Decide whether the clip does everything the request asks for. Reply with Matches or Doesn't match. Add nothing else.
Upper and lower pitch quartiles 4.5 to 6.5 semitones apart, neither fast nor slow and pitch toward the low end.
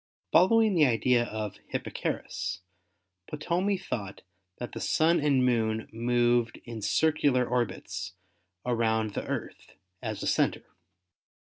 Doesn't match